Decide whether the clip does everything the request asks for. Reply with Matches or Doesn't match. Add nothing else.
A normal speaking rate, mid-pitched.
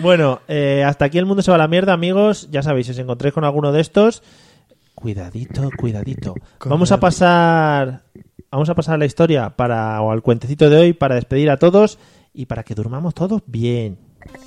Doesn't match